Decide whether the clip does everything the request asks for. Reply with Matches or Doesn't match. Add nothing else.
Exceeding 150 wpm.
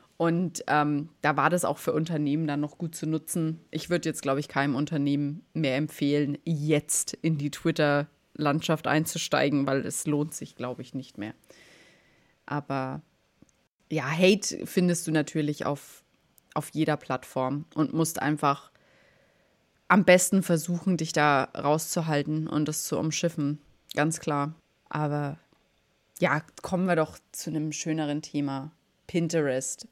Doesn't match